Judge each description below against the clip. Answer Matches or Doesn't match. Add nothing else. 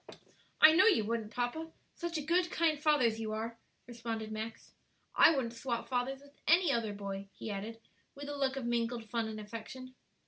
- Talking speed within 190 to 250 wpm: Matches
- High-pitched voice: Matches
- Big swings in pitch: Doesn't match